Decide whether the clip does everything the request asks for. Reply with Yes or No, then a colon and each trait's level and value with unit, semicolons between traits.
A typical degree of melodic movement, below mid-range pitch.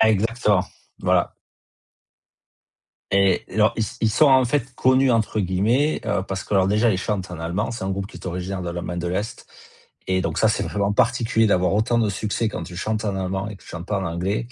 Yes: average, 3.2 semitones; low, 105 Hz